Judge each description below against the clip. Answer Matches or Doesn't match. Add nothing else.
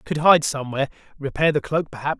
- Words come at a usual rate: Doesn't match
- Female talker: Doesn't match